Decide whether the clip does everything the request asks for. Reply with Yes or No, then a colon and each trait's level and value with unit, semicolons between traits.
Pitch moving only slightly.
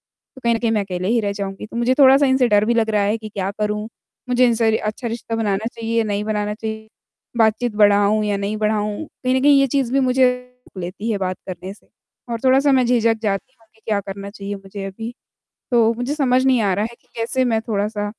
No: average, 3.0 semitones